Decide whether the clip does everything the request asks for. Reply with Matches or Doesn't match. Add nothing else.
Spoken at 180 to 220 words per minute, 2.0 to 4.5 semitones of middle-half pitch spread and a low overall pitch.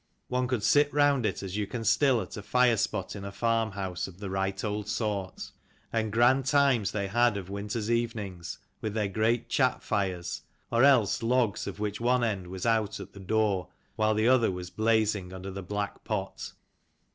Matches